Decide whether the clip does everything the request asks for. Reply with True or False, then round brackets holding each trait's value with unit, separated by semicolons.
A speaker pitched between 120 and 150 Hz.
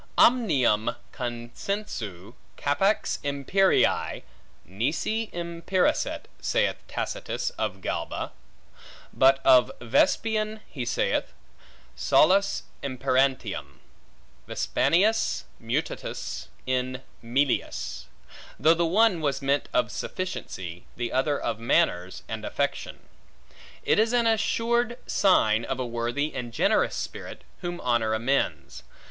True (140 Hz)